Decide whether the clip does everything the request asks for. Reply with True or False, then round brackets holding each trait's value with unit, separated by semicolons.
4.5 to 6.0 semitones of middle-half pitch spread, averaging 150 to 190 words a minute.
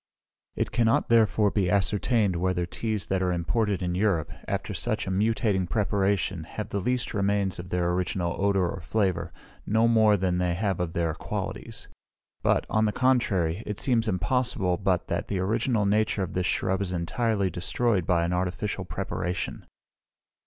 False (3.3 semitones; 165 wpm)